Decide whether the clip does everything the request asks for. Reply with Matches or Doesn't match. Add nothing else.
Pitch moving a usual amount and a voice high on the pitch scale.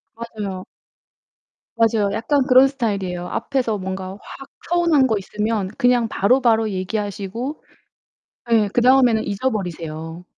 Matches